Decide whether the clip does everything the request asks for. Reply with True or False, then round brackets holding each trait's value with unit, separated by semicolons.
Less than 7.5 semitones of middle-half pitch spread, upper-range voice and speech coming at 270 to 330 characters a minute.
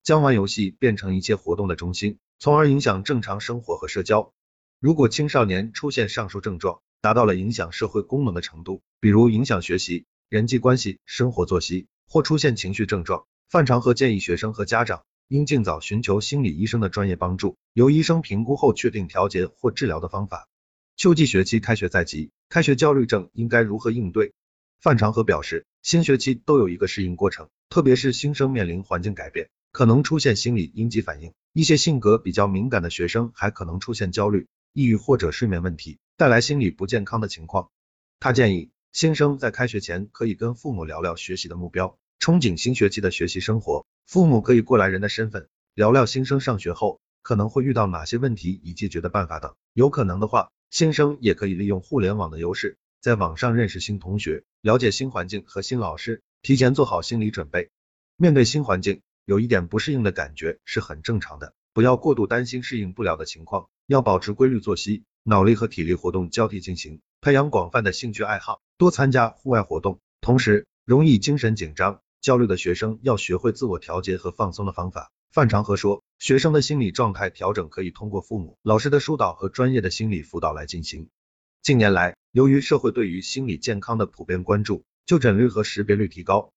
False (5.3 semitones; 110 Hz; 320 characters per minute)